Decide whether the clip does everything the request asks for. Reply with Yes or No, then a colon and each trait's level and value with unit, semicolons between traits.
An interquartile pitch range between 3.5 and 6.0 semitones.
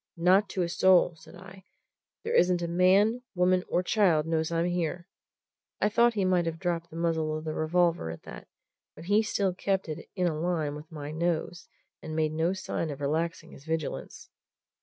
No: narrow, 2.6 semitones